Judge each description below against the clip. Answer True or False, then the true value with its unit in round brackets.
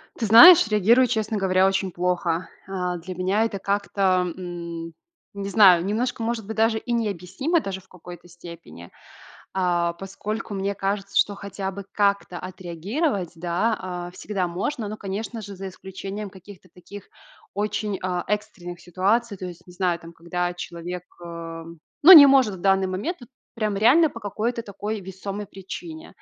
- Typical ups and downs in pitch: True (3.0 semitones)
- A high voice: True (195 Hz)